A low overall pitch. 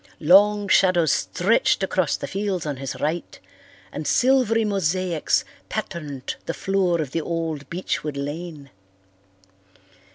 No: medium, 170 Hz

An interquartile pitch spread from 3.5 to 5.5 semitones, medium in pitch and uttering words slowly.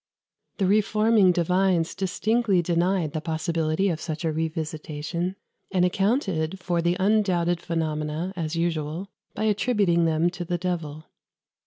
No: average, 3.1 semitones; medium, 175 Hz; slow, 130 wpm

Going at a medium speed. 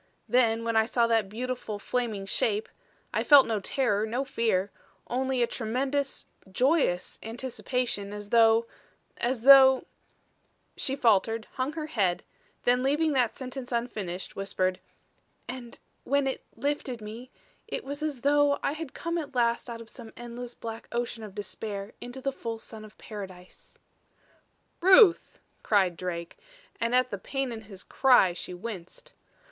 Yes: average, 150 wpm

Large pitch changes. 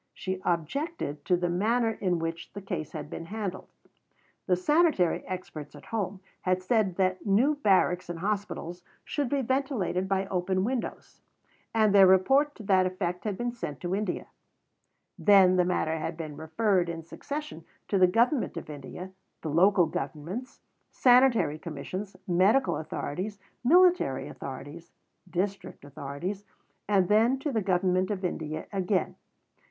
No: average, 4.1 semitones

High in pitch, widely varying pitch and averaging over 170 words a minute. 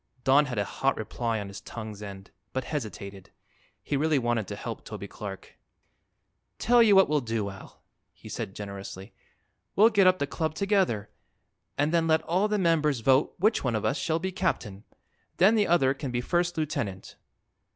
No: medium, 140 Hz; wide, 8.1 semitones; average, 180 wpm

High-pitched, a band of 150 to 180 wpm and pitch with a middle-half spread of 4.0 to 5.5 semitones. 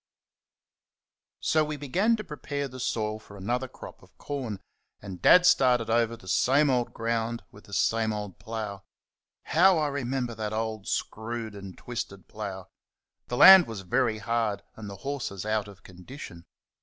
No: low, 115 Hz; average, 160 wpm; average, 4.3 semitones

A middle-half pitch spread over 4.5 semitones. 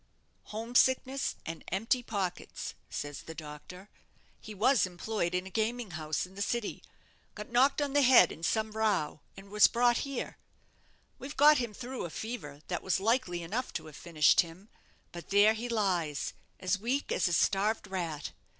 Yes: wide, 5.5 semitones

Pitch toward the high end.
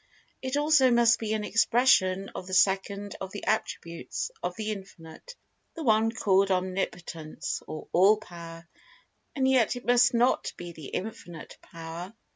Yes: high, 200 Hz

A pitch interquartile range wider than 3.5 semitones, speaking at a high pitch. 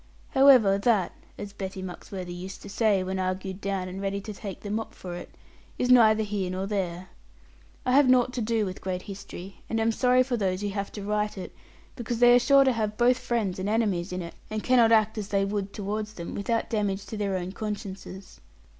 No: average, 2.9 semitones; high, 205 Hz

